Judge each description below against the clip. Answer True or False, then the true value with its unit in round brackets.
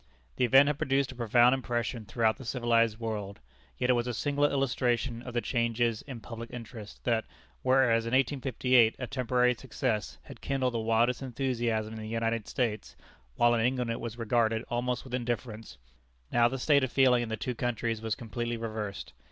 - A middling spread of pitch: False (1.9 semitones)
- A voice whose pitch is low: True (120 Hz)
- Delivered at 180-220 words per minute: True (185 wpm)